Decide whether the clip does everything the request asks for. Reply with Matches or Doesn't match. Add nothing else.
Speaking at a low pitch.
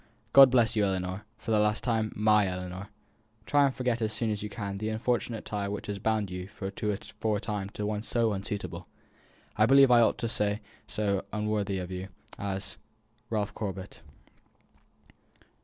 Matches